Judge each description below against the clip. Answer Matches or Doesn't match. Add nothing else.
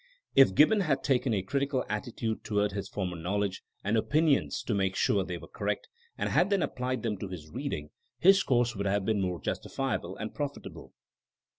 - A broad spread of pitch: Matches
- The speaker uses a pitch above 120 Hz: Doesn't match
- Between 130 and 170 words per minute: Doesn't match